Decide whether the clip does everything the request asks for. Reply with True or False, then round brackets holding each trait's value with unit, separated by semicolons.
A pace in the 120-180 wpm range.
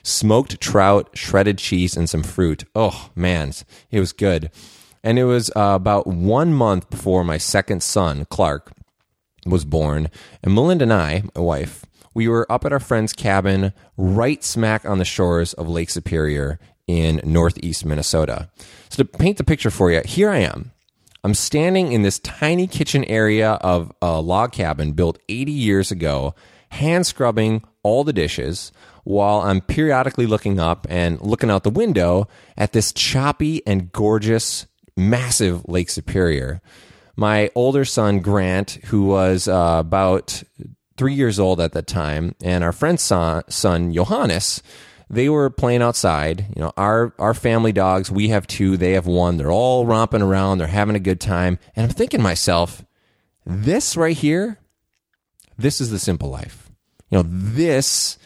True (165 wpm)